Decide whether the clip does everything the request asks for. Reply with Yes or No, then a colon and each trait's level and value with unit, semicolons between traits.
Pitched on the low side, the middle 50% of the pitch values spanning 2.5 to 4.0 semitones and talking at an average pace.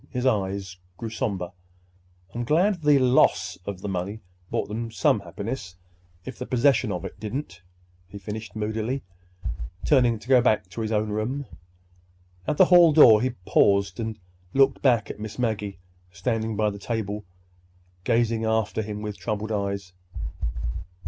Yes: low, 110 Hz; average, 3.5 semitones; average, 150 wpm